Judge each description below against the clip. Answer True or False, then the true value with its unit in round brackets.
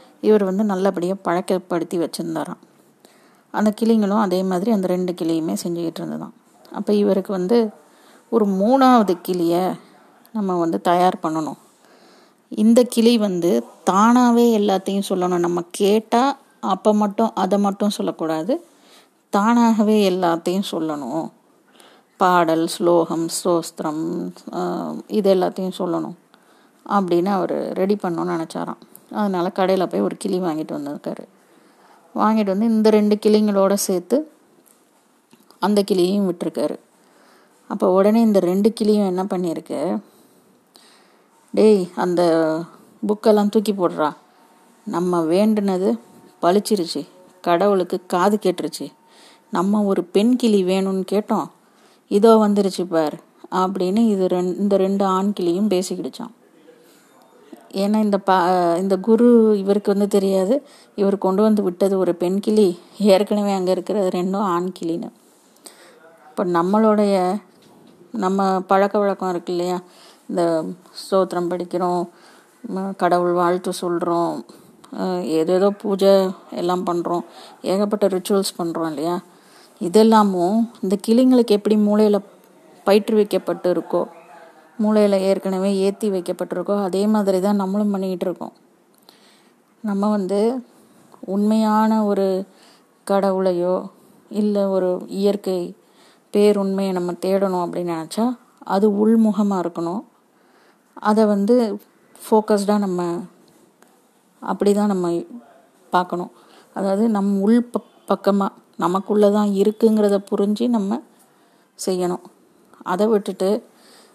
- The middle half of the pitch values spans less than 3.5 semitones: True (2.9 semitones)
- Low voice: False (195 Hz)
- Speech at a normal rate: True (105 wpm)